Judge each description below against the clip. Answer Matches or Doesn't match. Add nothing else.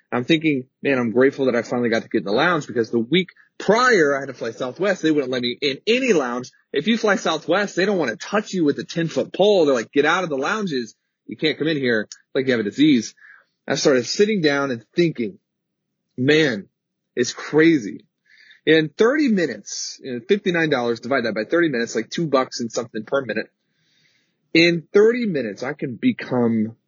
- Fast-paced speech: Matches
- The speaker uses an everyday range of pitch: Doesn't match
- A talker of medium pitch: Matches